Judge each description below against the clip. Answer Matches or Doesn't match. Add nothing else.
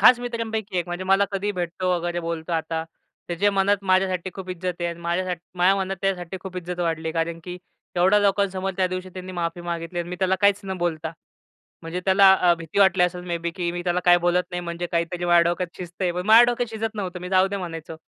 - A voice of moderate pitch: Matches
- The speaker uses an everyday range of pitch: Doesn't match